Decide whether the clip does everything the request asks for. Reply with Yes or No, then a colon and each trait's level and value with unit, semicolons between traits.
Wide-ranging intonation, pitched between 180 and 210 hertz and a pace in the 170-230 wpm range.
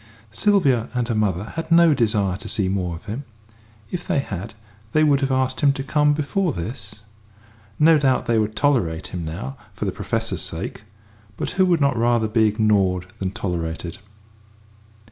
No: wide, 6.7 semitones; low, 115 Hz; average, 175 wpm